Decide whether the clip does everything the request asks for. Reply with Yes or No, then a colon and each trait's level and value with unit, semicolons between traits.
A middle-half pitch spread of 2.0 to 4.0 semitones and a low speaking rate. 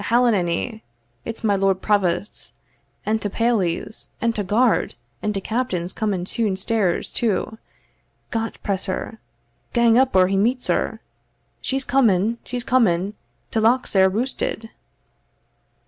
Yes: average, 3.6 semitones; slow, 130 wpm